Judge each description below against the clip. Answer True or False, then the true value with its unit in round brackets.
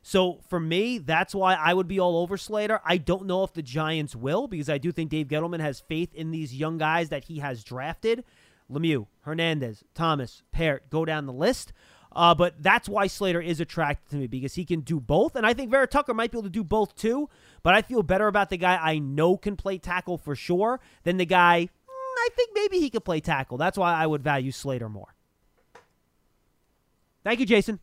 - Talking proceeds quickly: True (220 wpm)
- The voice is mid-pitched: True (175 Hz)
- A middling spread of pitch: True (4.8 semitones)